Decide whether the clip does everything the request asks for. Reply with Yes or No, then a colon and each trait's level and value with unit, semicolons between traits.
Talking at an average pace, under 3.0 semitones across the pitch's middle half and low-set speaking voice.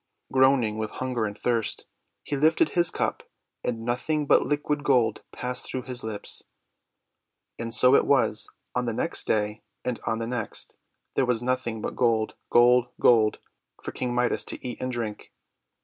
Yes: average, 165 wpm; narrow, 2.4 semitones; low, 125 Hz